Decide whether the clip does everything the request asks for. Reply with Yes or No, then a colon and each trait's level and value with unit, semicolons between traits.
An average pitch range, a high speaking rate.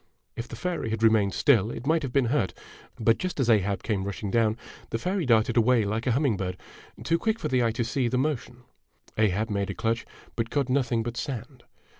Yes: average, 3.4 semitones; fast, 220 wpm